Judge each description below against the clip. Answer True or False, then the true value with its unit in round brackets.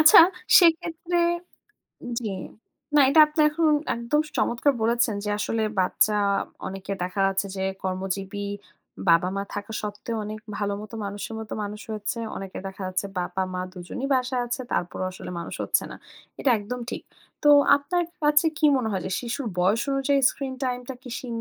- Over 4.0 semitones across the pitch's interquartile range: True (5.5 semitones)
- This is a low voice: False (220 Hz)